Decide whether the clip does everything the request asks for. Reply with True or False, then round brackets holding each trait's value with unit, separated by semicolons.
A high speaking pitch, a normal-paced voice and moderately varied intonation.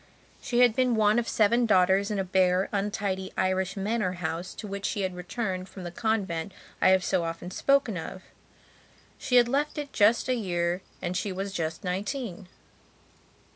True (195 Hz; 175 wpm; 3.5 semitones)